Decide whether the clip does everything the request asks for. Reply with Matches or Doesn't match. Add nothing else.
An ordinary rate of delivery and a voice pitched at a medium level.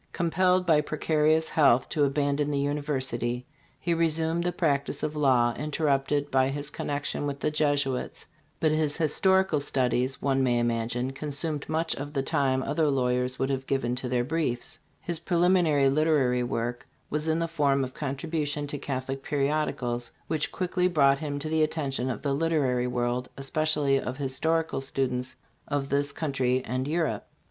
Matches